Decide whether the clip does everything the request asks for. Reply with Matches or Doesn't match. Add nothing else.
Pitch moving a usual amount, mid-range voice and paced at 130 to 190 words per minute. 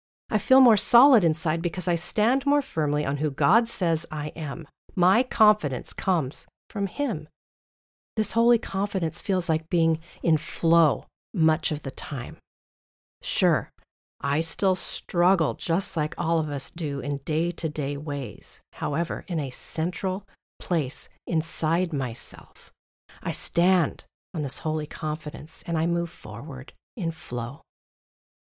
Matches